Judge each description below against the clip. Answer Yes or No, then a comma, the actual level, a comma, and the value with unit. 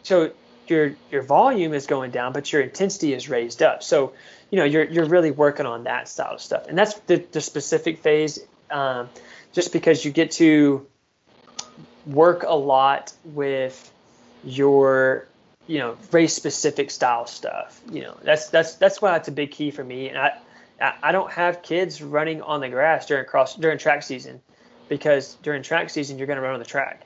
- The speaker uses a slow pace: No, average, 195 wpm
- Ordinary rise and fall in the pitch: Yes, average, 3.0 semitones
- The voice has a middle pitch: Yes, medium, 150 Hz